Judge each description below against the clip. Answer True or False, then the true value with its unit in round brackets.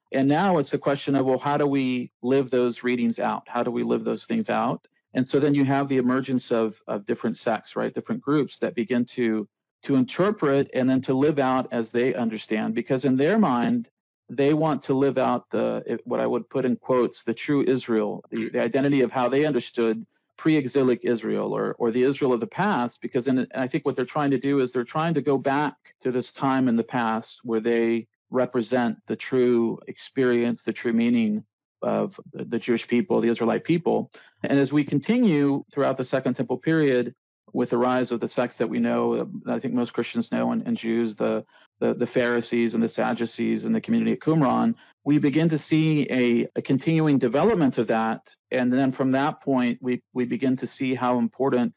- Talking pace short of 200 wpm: False (205 wpm)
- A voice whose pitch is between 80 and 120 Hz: False (130 Hz)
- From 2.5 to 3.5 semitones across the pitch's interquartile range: True (3.0 semitones)